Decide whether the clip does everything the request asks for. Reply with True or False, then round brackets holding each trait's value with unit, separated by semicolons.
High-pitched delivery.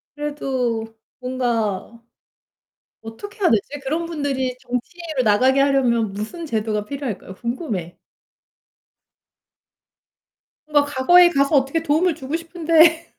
True (270 Hz)